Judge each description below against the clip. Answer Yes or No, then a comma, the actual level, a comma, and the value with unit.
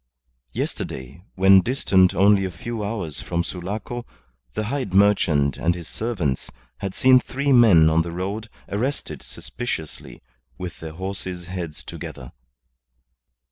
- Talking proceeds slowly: Yes, slow, 130 wpm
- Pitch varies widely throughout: No, average, 4.4 semitones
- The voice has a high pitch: No, very low, 95 Hz